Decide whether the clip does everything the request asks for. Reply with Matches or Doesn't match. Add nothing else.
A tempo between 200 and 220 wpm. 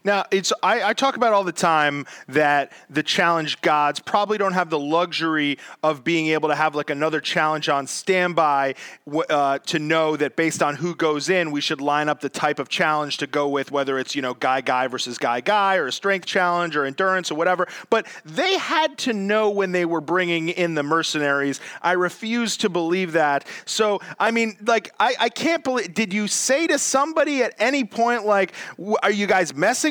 Matches